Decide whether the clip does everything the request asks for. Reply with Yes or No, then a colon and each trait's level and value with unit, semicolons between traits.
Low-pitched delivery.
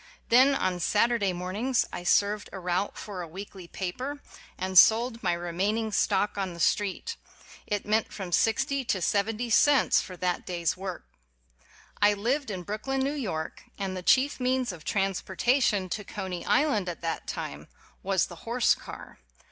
No: high, 200 Hz